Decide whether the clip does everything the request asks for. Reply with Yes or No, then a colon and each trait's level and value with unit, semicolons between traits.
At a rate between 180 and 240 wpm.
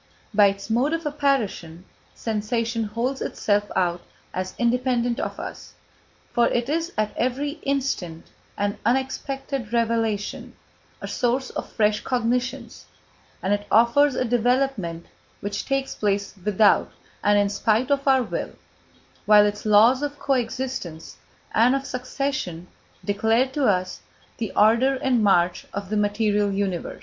No: average, 140 wpm